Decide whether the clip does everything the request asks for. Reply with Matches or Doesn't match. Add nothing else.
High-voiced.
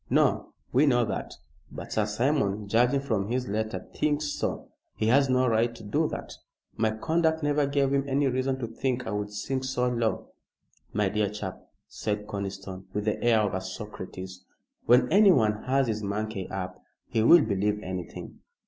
Doesn't match